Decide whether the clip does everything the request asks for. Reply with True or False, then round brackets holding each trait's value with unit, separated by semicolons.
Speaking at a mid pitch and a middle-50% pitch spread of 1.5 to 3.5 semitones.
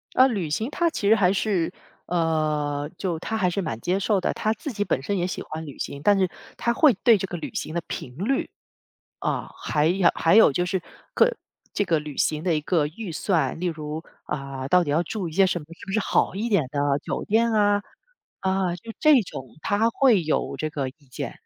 False (180 Hz; 4.9 semitones)